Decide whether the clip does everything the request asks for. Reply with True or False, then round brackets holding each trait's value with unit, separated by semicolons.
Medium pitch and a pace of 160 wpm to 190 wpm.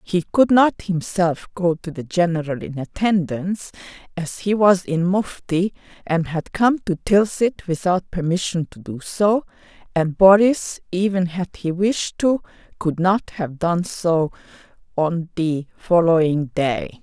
False (175 Hz; 145 wpm)